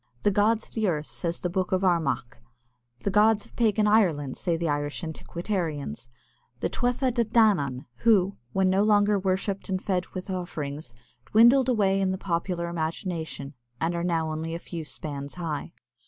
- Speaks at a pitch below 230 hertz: Yes, medium, 185 Hz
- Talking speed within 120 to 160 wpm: No, average, 170 wpm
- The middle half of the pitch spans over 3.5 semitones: Yes, average, 4.4 semitones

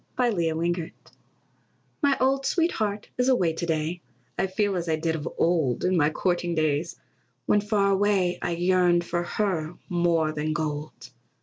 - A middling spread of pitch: Yes, average, 3.7 semitones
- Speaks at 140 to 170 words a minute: Yes, average, 165 wpm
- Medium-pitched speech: Yes, medium, 175 Hz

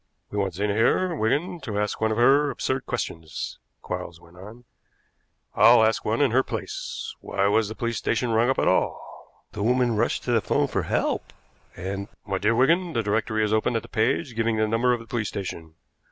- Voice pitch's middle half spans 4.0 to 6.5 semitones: No, average, 3.0 semitones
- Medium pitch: No, low, 110 Hz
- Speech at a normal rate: No, fast, 210 wpm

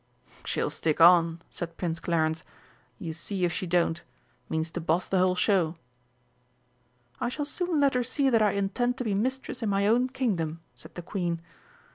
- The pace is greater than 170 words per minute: Yes, average, 180 wpm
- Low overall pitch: No, medium, 185 Hz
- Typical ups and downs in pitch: No, wide, 6.3 semitones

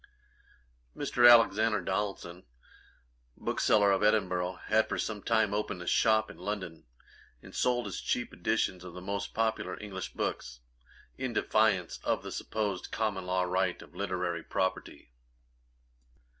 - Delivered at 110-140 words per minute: Yes, slow, 135 wpm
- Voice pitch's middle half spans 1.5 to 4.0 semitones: Yes, average, 3.2 semitones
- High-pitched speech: No, low, 100 Hz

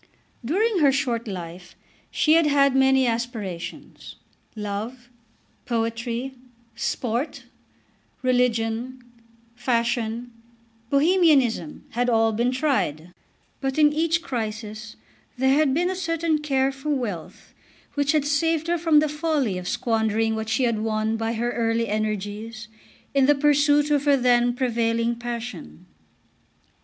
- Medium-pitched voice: No, high, 245 Hz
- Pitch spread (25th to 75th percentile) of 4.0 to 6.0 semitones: Yes, average, 4.3 semitones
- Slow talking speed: Yes, slow, 125 wpm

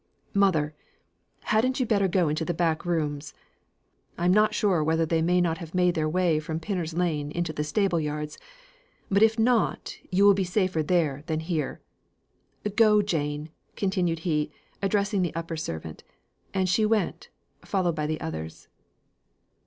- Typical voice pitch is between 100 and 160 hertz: No, medium, 170 Hz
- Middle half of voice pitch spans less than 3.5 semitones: No, average, 3.9 semitones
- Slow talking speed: No, average, 160 wpm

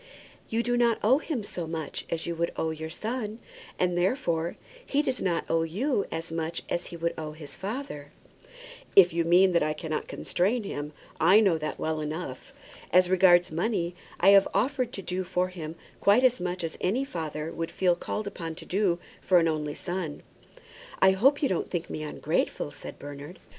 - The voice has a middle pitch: Yes, medium, 175 Hz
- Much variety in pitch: No, average, 3.8 semitones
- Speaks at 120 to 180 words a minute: No, average, 195 wpm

